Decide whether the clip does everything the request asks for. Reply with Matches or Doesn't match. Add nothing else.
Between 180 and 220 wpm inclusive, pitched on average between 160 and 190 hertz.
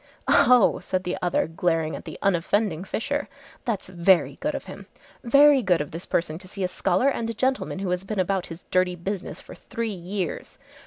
Matches